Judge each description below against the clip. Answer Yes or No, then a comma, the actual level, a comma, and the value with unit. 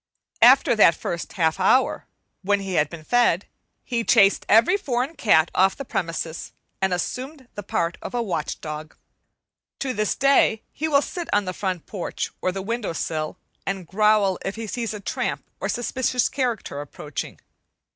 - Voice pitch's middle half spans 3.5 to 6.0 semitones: Yes, wide, 5.6 semitones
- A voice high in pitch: Yes, high, 205 Hz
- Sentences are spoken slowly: No, average, 170 wpm